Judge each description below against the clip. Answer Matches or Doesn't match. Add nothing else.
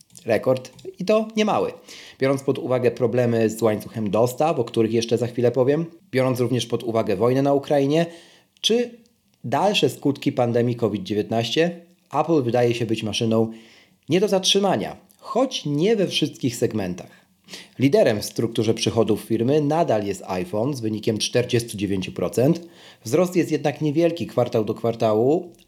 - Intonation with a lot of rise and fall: Matches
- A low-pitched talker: Matches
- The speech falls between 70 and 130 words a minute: Doesn't match